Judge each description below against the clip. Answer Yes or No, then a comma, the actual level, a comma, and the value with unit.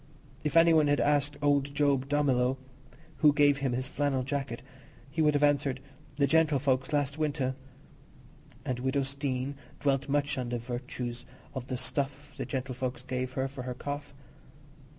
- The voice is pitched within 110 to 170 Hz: Yes, medium, 140 Hz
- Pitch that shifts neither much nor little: No, narrow, 2.0 semitones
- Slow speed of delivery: No, average, 160 wpm